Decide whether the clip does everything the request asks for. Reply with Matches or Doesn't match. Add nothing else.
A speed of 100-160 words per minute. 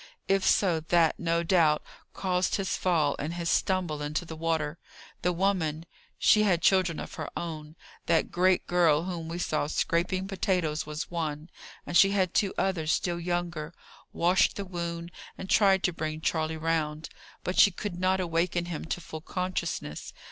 Doesn't match